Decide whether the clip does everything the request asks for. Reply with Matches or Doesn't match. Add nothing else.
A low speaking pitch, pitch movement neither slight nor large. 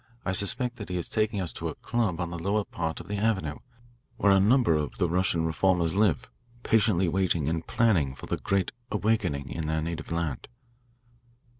Matches